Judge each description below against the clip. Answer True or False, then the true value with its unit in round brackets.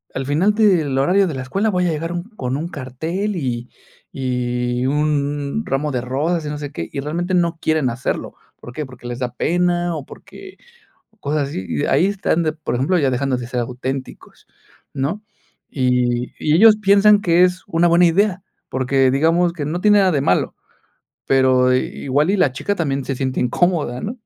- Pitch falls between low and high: True (150 Hz)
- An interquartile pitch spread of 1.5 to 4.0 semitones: False (5.3 semitones)